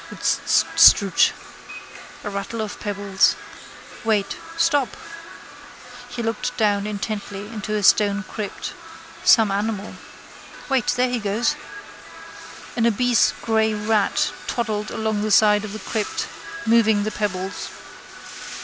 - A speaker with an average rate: No, slow, 115 wpm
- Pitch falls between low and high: No, high, 215 Hz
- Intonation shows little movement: Yes, narrow, 1.8 semitones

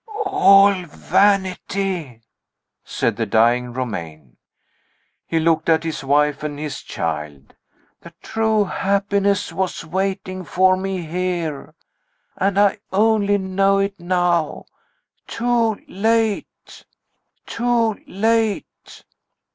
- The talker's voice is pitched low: No, medium, 185 Hz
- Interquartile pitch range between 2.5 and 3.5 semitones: No, average, 4.6 semitones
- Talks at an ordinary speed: No, slow, 100 wpm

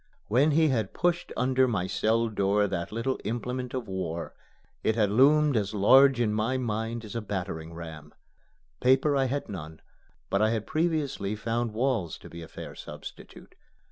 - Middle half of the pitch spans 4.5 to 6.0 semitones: Yes, average, 4.8 semitones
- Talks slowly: No, average, 170 wpm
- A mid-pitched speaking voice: No, low, 115 Hz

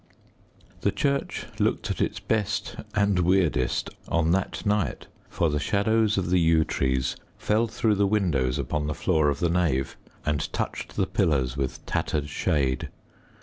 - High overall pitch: No, very low, 85 Hz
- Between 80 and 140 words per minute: No, average, 155 wpm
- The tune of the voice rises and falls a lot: Yes, wide, 5.9 semitones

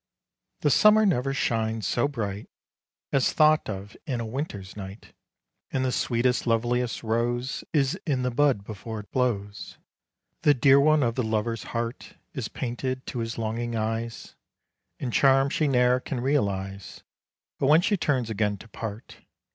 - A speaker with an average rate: Yes, average, 155 wpm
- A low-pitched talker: Yes, low, 120 Hz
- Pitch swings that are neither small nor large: Yes, average, 3.4 semitones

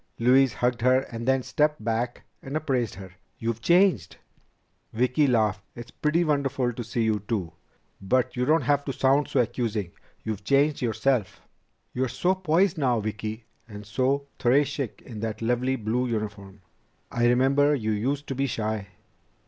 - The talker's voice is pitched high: No, low, 125 Hz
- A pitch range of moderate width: Yes, average, 4.0 semitones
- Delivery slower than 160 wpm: No, average, 165 wpm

